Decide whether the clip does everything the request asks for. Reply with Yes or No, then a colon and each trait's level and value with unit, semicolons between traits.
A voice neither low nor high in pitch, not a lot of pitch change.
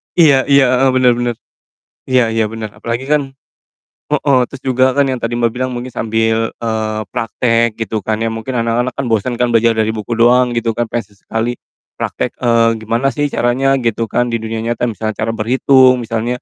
No: low, 115 Hz; narrow, 2.1 semitones